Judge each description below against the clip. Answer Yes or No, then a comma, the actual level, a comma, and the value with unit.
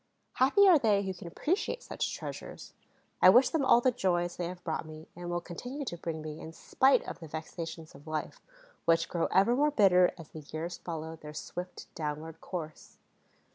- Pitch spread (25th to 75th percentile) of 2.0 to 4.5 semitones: No, average, 5.1 semitones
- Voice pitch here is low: No, medium, 175 Hz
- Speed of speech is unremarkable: Yes, average, 195 wpm